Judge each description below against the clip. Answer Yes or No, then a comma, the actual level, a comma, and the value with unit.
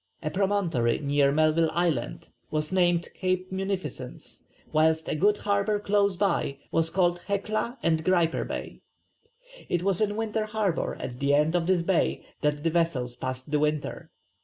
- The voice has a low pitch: No, medium, 170 Hz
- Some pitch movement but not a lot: Yes, average, 4.5 semitones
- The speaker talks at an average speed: Yes, average, 160 wpm